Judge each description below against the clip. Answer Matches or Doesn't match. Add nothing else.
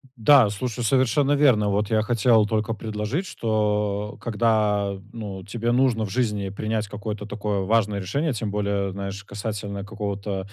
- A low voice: Matches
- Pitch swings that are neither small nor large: Doesn't match